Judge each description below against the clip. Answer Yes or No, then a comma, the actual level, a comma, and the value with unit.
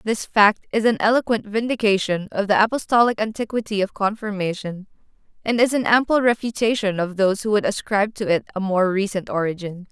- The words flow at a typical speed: Yes, average, 170 wpm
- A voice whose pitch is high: Yes, high, 210 Hz